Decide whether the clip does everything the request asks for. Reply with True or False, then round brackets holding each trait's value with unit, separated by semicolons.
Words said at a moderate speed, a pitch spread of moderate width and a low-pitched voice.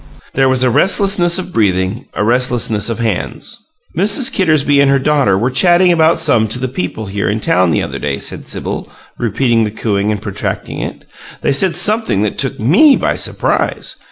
False (185 wpm; 7.8 semitones; 125 Hz)